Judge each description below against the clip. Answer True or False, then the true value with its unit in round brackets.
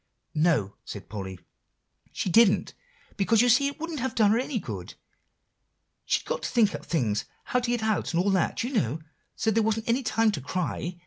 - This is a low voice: False (215 Hz)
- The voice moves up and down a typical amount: False (6.3 semitones)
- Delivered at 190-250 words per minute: True (195 wpm)